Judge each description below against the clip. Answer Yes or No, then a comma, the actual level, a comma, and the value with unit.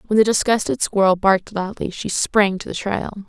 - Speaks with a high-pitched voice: Yes, high, 200 Hz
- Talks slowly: No, average, 200 wpm